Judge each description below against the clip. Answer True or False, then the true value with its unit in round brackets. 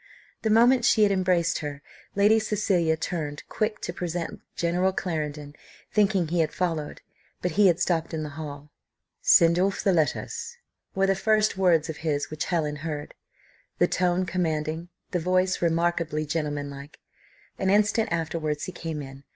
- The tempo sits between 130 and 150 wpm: False (160 wpm)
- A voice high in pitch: False (170 Hz)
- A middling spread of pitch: True (3.7 semitones)